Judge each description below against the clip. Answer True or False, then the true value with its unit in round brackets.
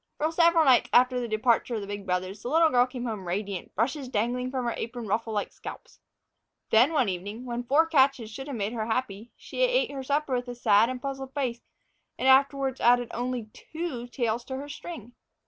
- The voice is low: False (245 Hz)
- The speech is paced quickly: True (210 wpm)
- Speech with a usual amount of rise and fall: True (3.5 semitones)